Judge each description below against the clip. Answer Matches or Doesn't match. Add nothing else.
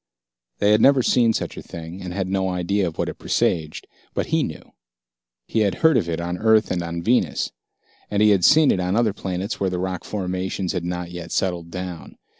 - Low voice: Matches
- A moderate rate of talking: Doesn't match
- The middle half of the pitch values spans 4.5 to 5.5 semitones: Doesn't match